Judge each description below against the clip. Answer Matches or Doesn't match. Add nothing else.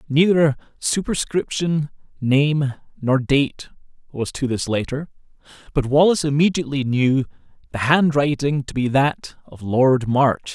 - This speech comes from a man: Matches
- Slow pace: Matches